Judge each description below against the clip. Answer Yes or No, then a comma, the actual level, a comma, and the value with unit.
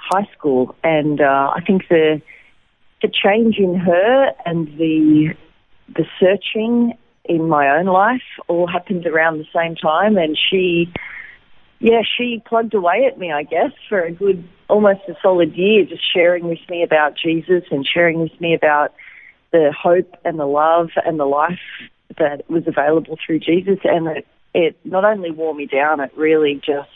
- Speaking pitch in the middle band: Yes, medium, 170 Hz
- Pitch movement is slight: No, average, 3.5 semitones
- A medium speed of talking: Yes, average, 170 wpm